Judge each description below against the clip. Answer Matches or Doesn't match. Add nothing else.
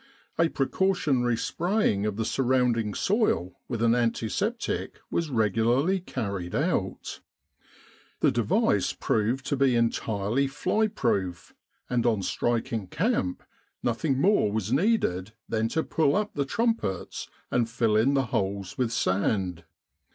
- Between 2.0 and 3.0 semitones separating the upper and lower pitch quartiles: Doesn't match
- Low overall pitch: Matches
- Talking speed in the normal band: Doesn't match